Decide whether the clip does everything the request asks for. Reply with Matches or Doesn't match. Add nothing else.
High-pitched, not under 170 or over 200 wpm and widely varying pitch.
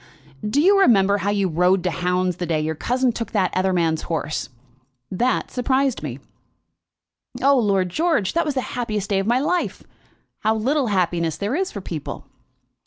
Matches